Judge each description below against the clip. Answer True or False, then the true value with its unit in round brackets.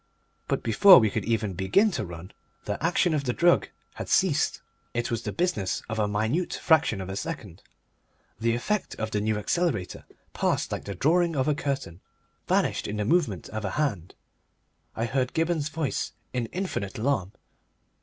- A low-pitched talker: True (120 Hz)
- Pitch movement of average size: False (7.6 semitones)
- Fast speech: False (175 wpm)